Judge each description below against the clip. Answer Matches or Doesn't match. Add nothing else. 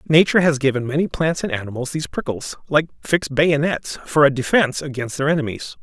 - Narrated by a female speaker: Doesn't match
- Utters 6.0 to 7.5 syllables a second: Matches